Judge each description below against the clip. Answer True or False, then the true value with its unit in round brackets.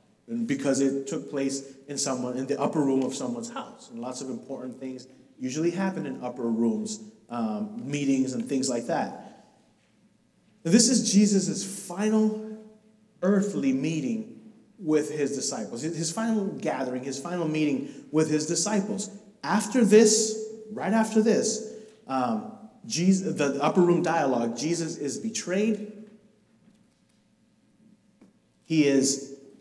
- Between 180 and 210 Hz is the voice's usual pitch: True (185 Hz)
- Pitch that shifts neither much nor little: False (7.9 semitones)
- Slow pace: True (130 wpm)